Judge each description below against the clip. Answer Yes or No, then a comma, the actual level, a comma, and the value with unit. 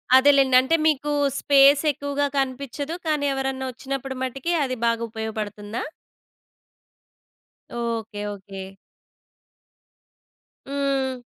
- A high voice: Yes, very high, 265 Hz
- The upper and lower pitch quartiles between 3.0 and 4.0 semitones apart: Yes, average, 3.3 semitones